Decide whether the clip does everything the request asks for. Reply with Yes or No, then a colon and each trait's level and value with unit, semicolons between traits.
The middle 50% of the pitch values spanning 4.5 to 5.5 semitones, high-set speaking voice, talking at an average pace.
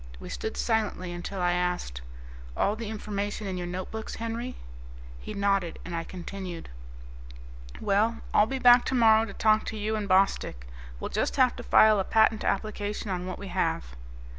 No: average, 3.4 semitones; high, 200 Hz; average, 170 wpm